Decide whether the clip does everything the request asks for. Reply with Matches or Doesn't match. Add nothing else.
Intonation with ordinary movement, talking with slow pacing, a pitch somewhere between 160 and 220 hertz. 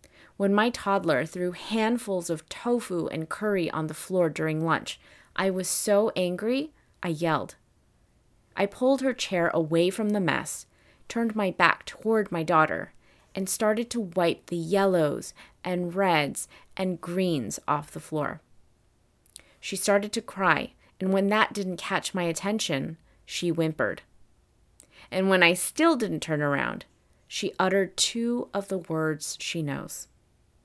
Doesn't match